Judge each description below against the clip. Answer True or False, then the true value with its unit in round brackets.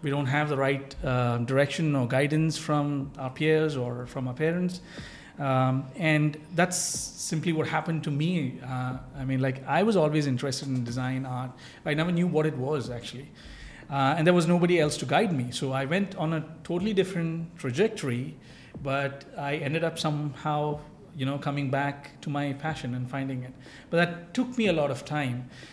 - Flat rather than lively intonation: False (3.3 semitones)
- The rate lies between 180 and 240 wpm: True (190 wpm)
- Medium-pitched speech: True (145 Hz)